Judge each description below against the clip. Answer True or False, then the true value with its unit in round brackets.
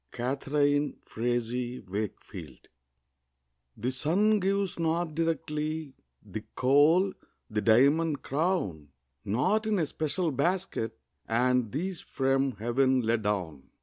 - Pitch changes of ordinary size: False (5.9 semitones)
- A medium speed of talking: False (105 wpm)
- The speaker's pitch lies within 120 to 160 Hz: True (135 Hz)